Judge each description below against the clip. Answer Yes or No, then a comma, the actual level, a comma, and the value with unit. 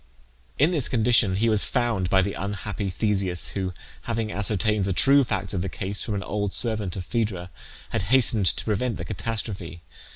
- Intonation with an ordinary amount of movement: Yes, average, 3.2 semitones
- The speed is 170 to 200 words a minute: Yes, average, 185 wpm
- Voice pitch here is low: Yes, low, 105 Hz